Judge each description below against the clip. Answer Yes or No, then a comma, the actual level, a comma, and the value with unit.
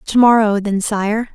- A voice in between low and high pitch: No, high, 215 Hz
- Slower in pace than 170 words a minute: Yes, slow, 135 wpm